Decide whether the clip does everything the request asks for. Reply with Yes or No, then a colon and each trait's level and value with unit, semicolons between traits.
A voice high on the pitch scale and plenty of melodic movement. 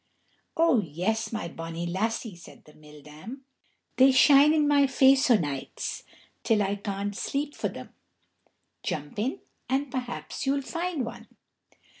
Yes: high, 225 Hz; wide, 7.9 semitones